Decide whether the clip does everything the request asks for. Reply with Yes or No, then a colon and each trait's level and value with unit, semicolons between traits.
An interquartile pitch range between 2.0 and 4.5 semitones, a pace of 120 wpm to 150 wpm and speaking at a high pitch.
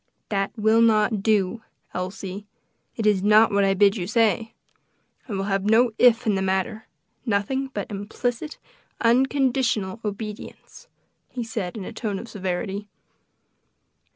Yes: average, 2.7 semitones; average, 140 wpm; high, 210 Hz